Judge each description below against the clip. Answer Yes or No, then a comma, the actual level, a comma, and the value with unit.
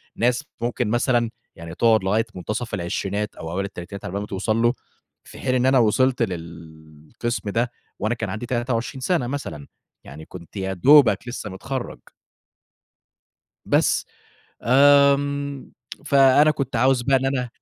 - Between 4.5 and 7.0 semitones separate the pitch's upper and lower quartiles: Yes, average, 5.2 semitones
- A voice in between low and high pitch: No, low, 120 Hz